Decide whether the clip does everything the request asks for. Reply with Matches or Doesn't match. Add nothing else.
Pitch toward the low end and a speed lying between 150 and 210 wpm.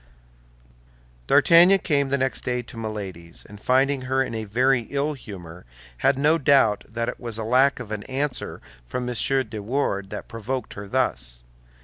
Matches